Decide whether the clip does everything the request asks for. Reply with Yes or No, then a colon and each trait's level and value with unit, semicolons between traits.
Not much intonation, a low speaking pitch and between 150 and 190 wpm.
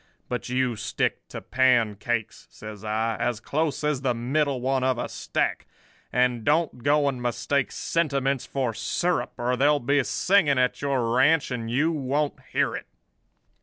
No: average, 3.1 semitones; low, 130 Hz; average, 160 wpm